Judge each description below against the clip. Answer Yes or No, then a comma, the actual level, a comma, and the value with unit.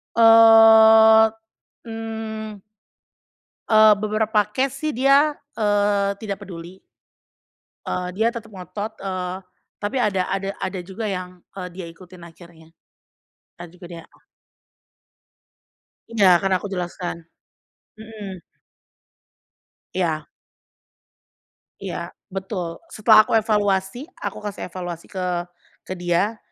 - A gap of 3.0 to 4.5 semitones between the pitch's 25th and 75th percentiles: Yes, average, 3.4 semitones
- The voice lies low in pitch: No, high, 205 Hz